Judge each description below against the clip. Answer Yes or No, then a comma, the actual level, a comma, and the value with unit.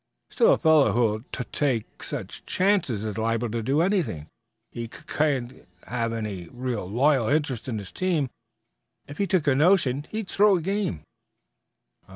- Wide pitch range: Yes, wide, 6.4 semitones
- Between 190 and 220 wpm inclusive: No, average, 165 wpm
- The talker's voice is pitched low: Yes, low, 130 Hz